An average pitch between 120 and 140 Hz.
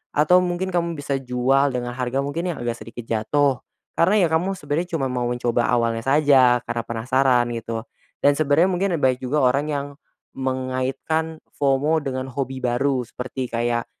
Yes: low, 135 Hz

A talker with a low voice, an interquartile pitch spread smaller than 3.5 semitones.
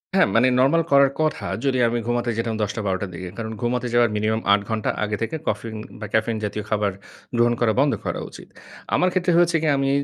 No: low, 115 Hz; average, 4.0 semitones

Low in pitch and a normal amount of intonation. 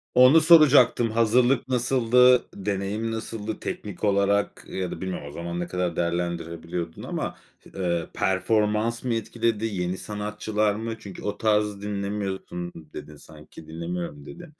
Yes: low, 105 Hz; average, 4.3 semitones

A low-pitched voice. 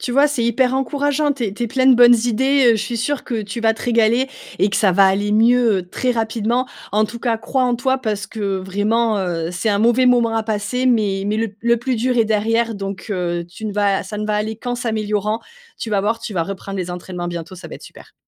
No: high, 220 Hz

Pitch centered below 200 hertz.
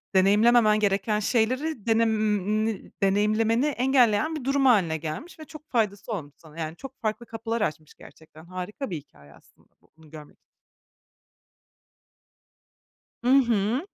No: high, 215 Hz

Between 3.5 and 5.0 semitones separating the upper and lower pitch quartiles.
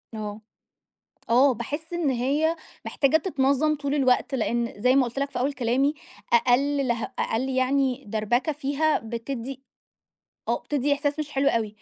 No: average, 3.1 semitones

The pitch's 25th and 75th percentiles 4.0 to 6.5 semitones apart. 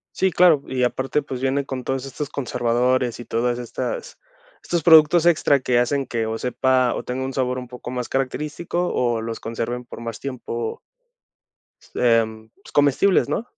No: average, 2.8 semitones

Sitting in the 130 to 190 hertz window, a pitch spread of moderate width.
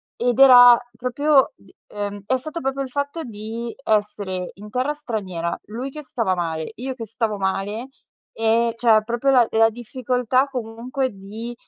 No: high, 235 Hz; average, 3.6 semitones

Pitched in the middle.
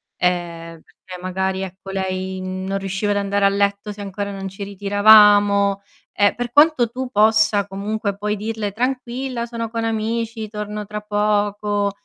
No: high, 205 Hz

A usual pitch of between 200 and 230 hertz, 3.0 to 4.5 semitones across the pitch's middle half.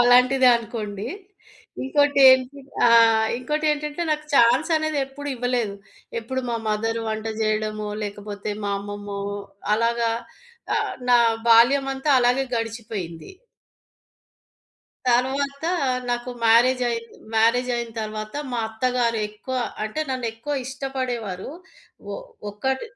No: high, 240 Hz; average, 3.5 semitones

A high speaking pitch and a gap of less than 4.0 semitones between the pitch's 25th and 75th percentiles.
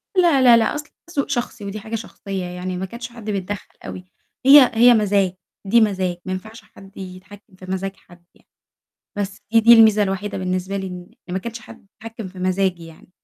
Yes: high, 200 Hz; average, 3.4 semitones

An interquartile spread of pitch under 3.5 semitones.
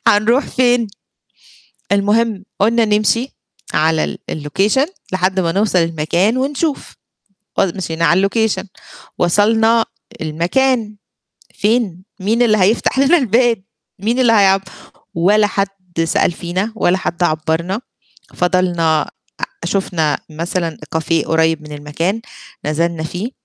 No: average, 5.1 semitones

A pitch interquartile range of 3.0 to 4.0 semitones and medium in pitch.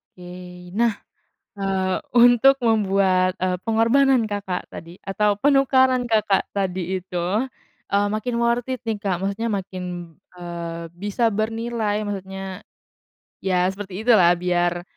No: average, 3.7 semitones; high, 200 Hz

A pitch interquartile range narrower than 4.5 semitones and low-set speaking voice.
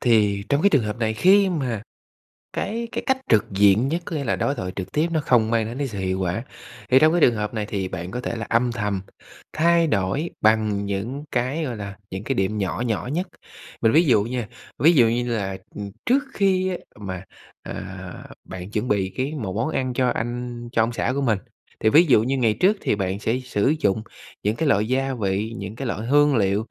No: average, 5.2 semitones; low, 115 Hz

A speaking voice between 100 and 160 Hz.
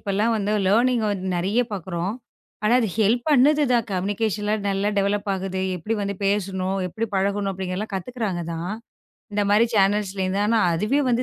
No: high, 205 Hz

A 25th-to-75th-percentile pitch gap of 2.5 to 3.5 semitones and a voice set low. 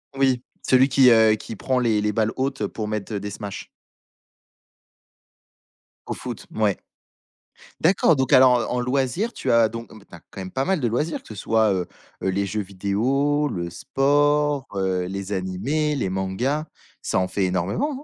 No: wide, 5.6 semitones; low, 115 Hz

